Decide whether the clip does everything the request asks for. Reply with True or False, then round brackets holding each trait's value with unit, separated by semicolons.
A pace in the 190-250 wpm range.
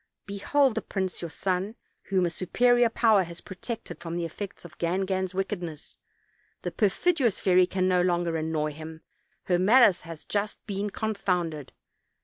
False (155 wpm)